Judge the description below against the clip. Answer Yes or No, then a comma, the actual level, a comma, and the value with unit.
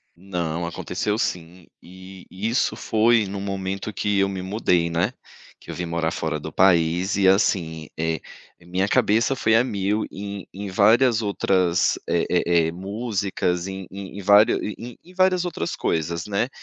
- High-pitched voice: No, very low, 95 Hz